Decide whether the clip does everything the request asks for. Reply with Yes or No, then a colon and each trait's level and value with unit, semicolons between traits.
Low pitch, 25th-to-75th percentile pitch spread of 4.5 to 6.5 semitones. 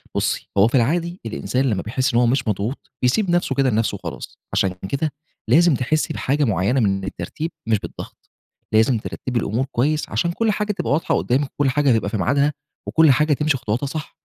Yes: low, 130 Hz; average, 5.2 semitones